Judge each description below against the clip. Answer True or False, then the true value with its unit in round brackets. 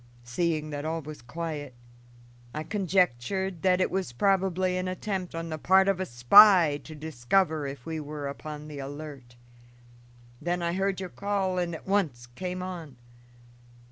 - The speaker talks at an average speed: True (160 wpm)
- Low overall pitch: False (165 Hz)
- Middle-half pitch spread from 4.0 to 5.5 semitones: True (4.3 semitones)